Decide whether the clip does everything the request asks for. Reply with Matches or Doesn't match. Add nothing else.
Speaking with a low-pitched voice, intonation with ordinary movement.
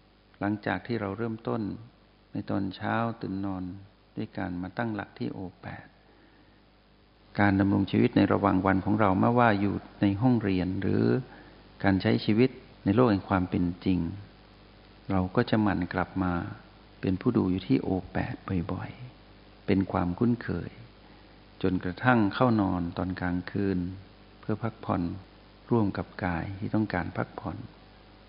Doesn't match